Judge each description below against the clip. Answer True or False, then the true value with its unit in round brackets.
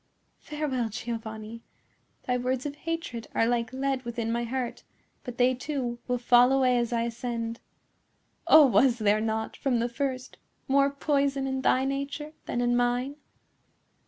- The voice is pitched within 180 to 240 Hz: False (250 Hz)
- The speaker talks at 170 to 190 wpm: False (155 wpm)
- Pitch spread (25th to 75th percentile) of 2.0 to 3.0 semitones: True (2.4 semitones)